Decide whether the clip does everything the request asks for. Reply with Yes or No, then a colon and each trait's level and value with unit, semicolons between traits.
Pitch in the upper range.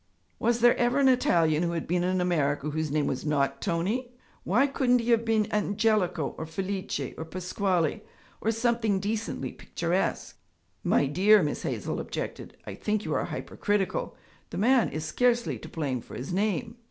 Yes: high, 195 Hz